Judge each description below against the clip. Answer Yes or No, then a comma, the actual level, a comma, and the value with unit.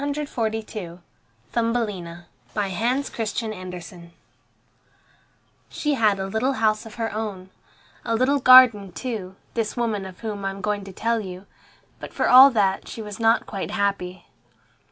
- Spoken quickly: No, average, 145 wpm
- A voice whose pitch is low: No, high, 215 Hz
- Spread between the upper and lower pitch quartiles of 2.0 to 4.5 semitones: Yes, average, 3.3 semitones